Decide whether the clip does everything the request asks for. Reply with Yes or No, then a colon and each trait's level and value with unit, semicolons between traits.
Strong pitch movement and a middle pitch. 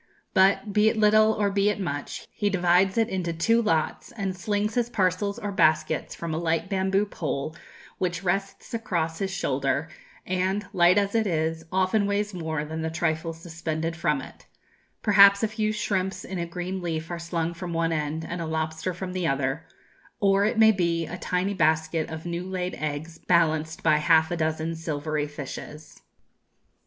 No: average, 3.7 semitones; medium, 175 Hz